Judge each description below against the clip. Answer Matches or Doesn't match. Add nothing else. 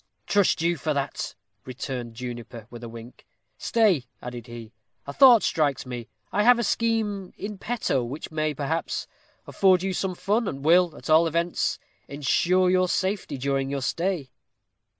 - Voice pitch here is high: Doesn't match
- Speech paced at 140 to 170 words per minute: Matches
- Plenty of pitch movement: Matches